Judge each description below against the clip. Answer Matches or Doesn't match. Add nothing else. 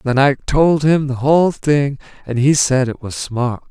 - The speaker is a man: Matches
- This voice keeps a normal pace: Doesn't match